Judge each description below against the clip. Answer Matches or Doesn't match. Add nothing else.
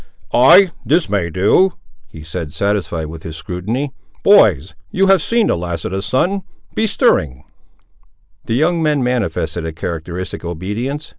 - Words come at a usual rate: Matches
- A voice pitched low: Matches